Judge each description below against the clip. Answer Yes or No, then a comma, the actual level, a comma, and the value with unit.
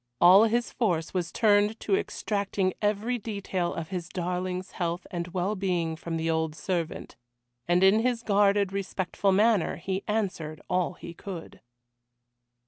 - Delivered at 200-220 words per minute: No, average, 145 wpm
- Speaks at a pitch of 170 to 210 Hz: Yes, high, 190 Hz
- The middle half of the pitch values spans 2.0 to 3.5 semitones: Yes, average, 3.0 semitones